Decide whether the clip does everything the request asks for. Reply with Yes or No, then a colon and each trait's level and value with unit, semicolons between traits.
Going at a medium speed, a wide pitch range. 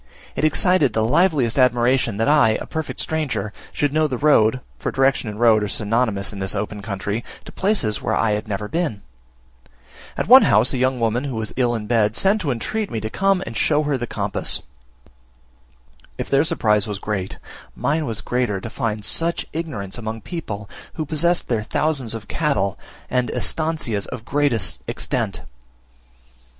Yes: average, 175 wpm; wide, 5.8 semitones